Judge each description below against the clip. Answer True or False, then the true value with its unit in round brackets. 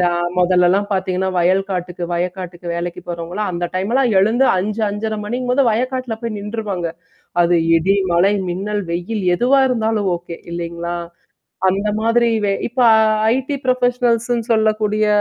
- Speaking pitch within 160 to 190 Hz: False (205 Hz)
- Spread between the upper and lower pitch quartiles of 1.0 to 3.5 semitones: False (4.5 semitones)